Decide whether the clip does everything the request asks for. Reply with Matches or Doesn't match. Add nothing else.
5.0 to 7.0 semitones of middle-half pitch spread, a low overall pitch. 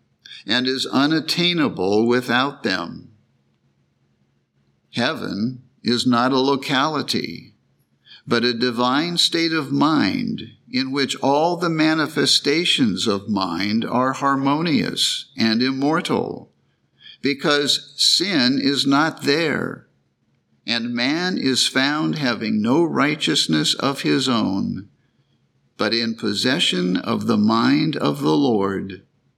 Doesn't match